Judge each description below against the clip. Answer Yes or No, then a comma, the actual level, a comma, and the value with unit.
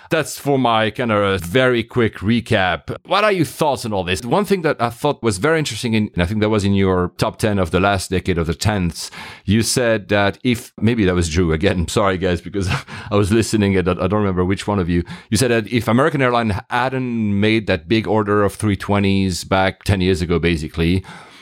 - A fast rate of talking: Yes, fast, 230 wpm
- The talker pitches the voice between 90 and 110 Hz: Yes, low, 105 Hz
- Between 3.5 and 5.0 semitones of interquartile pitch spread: Yes, average, 3.8 semitones